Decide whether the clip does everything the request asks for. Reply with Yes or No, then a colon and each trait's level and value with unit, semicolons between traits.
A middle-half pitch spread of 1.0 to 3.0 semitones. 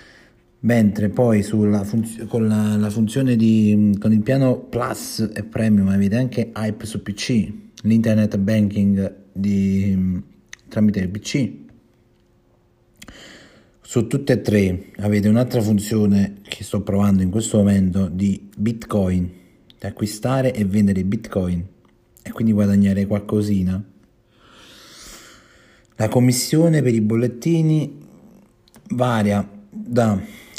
Yes: average, 2.7 semitones